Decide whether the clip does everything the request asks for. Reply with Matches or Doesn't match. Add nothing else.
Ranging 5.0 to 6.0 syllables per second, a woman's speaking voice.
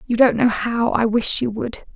Doesn't match